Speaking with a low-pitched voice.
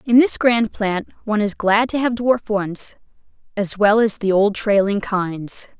No: high, 210 Hz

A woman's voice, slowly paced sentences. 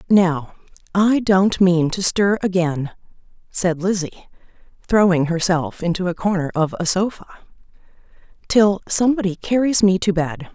Yes: female; slow, 130 wpm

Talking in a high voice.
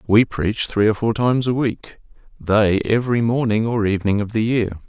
No: low, 110 Hz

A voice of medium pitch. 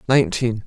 No: low, 125 Hz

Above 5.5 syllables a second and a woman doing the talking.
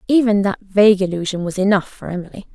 Yes: 6.4 syllables/s; female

